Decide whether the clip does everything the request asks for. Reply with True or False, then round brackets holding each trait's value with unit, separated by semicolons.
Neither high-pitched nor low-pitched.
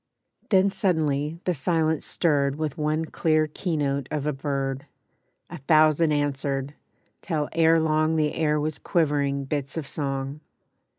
True (150 Hz)